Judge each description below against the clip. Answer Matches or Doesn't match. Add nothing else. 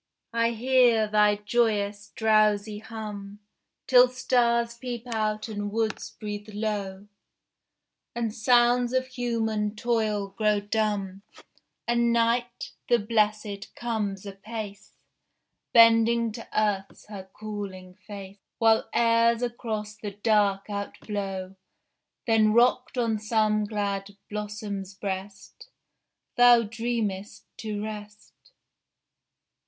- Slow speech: Matches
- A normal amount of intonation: Doesn't match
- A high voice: Matches